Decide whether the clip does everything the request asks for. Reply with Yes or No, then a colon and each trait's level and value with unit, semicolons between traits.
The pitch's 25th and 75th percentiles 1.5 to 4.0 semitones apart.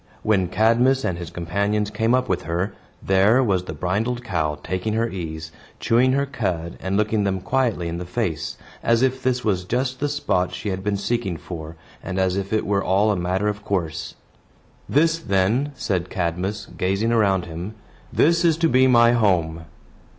No: average, 4.6 semitones